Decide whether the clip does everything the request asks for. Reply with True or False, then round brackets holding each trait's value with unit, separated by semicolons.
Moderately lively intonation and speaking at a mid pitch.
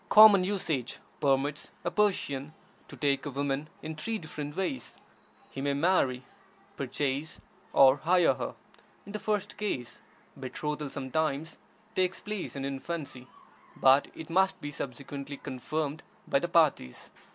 True (4.0 semitones; 145 Hz)